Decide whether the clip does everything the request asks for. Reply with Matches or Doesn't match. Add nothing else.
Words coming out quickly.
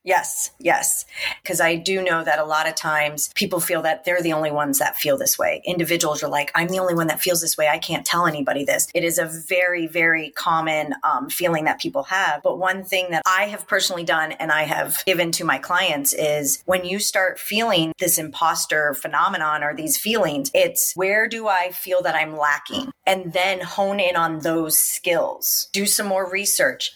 Matches